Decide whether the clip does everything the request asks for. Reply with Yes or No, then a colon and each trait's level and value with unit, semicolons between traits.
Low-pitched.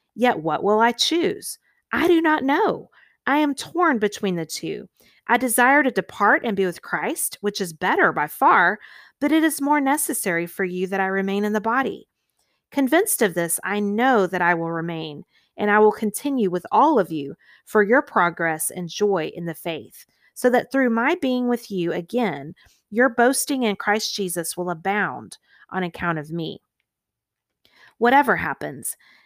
No: high, 210 Hz